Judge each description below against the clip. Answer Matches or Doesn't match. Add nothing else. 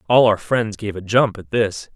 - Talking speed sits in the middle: Doesn't match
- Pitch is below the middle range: Matches